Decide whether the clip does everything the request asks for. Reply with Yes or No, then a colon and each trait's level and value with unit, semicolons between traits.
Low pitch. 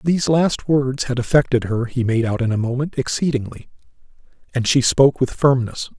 Yes: low, 130 Hz